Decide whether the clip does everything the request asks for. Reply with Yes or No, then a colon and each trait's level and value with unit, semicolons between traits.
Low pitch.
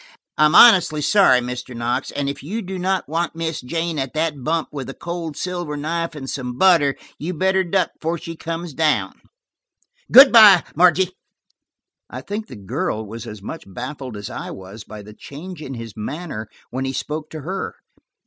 No: medium, 155 Hz